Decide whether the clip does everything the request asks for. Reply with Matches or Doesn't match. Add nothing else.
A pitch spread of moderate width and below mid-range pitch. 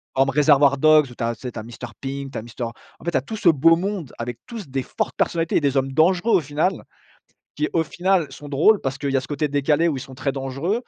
Doesn't match